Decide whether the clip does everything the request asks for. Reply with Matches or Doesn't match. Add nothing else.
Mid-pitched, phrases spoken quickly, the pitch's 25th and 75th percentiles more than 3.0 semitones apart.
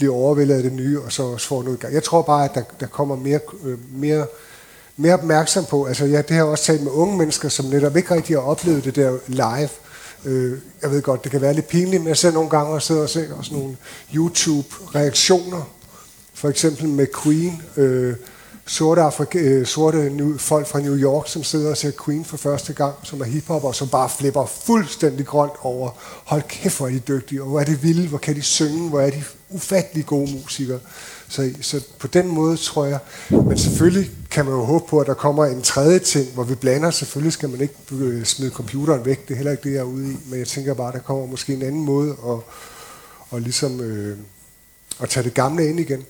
Doesn't match